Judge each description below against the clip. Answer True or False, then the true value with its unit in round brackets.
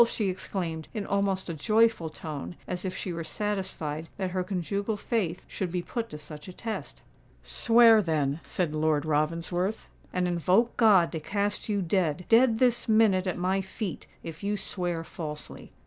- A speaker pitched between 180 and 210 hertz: True (185 Hz)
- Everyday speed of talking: True (165 wpm)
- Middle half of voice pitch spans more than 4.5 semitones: False (4.1 semitones)